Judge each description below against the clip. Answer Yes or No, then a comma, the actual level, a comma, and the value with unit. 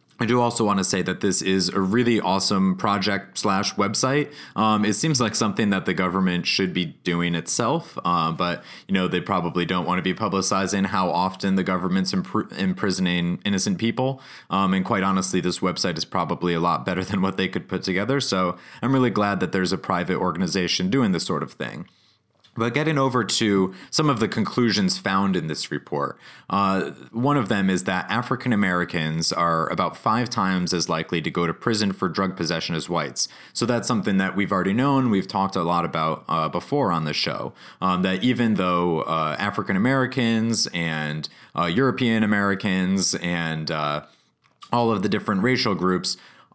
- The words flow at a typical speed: Yes, average, 190 wpm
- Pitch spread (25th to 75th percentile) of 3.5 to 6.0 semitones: Yes, average, 4.0 semitones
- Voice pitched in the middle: No, very low, 95 Hz